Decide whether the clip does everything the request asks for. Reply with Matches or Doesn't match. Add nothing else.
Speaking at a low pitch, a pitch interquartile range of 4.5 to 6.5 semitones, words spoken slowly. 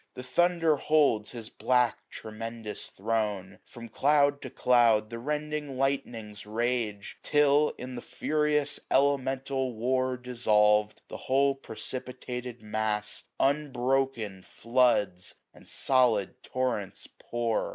Doesn't match